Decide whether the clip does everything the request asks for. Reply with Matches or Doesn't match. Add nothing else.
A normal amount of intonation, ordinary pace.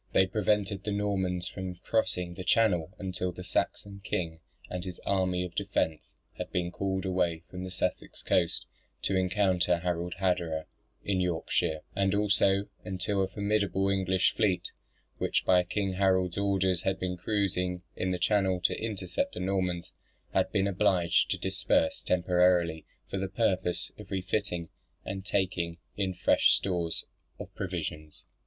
Doesn't match